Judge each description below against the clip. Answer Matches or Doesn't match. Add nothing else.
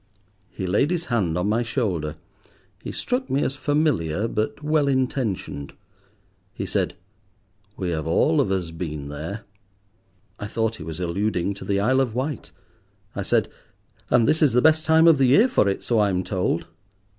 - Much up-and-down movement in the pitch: Matches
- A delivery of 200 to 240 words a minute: Doesn't match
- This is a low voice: Matches